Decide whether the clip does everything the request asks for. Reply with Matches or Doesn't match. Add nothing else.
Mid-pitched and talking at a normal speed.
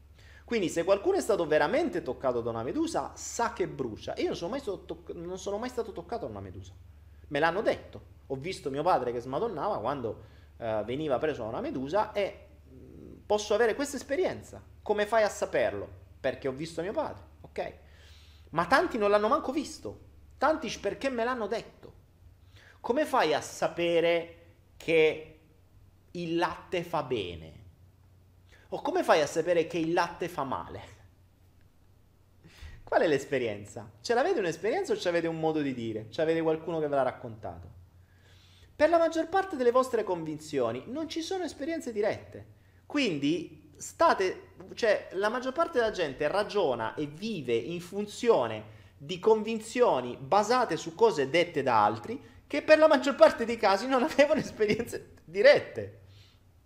Matches